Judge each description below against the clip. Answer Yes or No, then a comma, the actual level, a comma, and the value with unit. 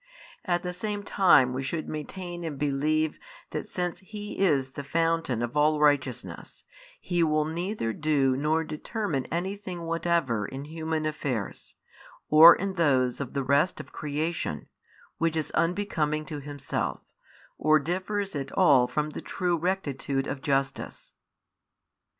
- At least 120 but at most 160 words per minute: Yes, average, 140 wpm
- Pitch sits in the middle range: Yes, medium, 155 Hz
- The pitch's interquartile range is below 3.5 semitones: No, average, 3.8 semitones